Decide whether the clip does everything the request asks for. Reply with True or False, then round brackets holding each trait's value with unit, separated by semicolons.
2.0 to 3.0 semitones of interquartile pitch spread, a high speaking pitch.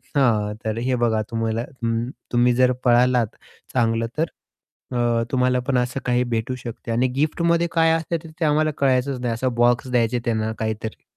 False (2.6 semitones; 125 Hz)